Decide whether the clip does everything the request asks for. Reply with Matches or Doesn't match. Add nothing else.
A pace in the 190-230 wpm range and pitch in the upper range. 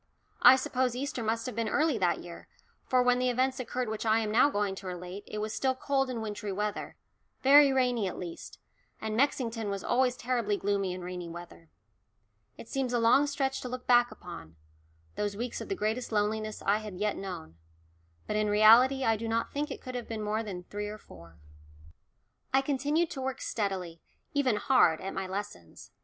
Matches